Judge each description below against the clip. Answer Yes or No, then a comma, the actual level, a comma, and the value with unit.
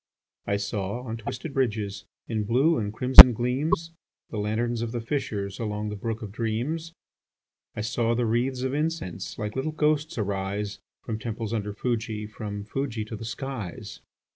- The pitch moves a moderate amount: Yes, average, 3.5 semitones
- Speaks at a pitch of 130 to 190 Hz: No, low, 115 Hz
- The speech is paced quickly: No, average, 165 wpm